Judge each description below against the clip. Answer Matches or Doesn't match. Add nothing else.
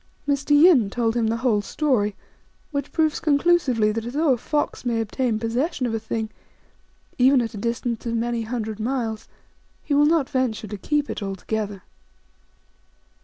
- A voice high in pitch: Matches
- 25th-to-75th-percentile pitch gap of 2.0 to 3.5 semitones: Doesn't match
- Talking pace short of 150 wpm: Doesn't match